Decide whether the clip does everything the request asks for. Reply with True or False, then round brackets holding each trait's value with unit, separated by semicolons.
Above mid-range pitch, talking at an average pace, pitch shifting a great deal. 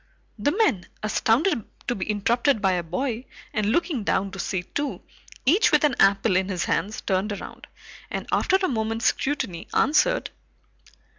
True (220 Hz; 160 wpm; 6.7 semitones)